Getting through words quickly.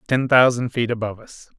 No: average, 190 wpm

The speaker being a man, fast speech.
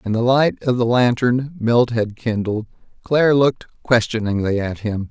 No: male; average, 165 wpm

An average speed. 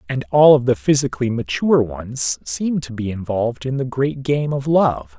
Yes: average, 195 wpm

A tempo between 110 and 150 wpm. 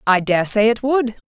No: fast, 235 wpm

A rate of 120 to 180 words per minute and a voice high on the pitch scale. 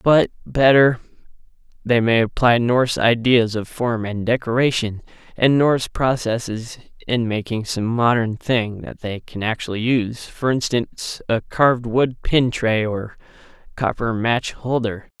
No: average, 140 wpm; low, 115 Hz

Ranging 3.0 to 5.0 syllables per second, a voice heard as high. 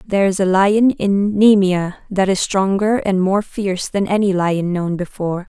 Yes: 4.6 syllables/s; high, 195 Hz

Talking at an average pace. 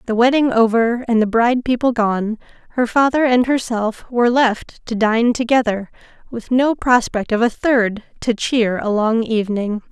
Yes: average, 170 wpm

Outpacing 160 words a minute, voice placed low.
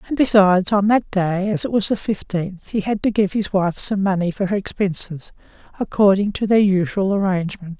No: average, 200 wpm; high, 195 Hz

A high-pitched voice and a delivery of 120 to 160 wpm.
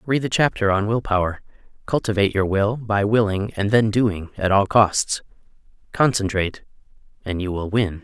No: low, 105 Hz; average, 155 wpm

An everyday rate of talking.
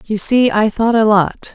No: fast, 235 wpm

